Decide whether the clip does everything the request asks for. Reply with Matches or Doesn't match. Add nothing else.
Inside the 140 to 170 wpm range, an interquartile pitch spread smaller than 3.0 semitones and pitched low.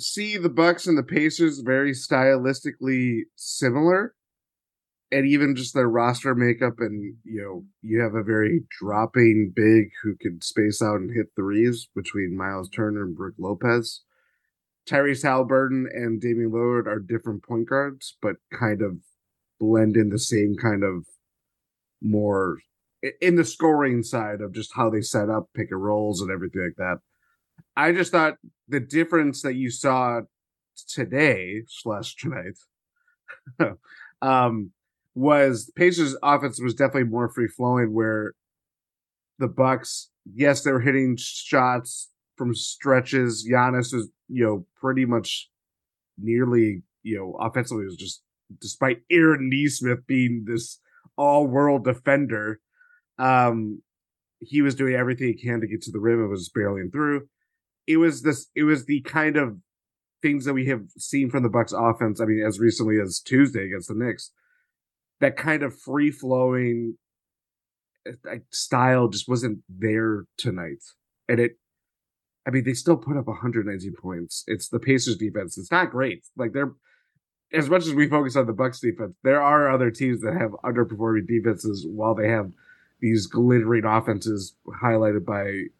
Doesn't match